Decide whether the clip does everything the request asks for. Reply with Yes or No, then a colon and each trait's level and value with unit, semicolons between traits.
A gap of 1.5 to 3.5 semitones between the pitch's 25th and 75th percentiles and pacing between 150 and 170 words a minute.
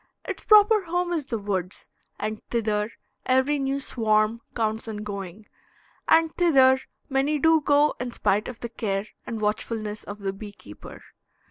No: average, 5.2 semitones; average, 155 wpm